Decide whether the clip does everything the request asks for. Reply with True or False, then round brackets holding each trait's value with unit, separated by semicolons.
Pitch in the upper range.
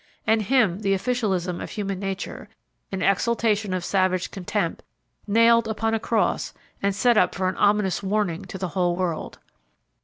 True (195 Hz)